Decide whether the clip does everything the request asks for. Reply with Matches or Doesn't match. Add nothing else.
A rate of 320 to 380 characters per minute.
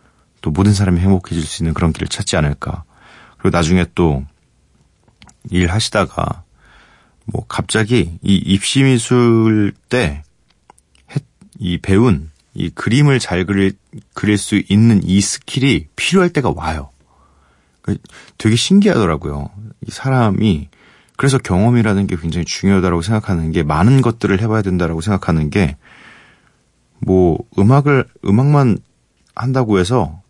Doesn't match